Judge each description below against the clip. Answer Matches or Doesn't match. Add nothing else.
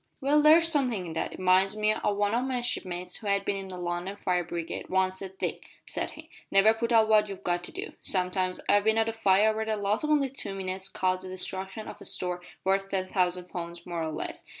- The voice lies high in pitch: Matches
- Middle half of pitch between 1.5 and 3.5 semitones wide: Matches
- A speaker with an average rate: Doesn't match